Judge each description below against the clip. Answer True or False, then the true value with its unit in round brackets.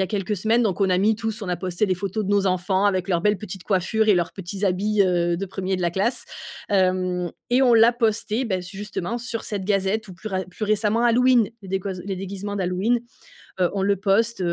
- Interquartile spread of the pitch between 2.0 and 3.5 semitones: True (2.8 semitones)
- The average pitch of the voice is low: False (195 Hz)